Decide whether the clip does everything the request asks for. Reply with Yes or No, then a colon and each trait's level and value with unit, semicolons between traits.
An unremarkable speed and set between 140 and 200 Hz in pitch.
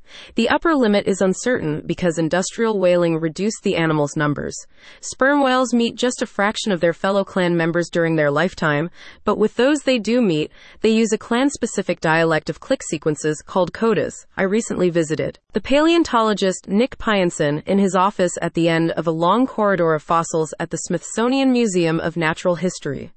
Yes: average, 180 wpm; medium, 185 Hz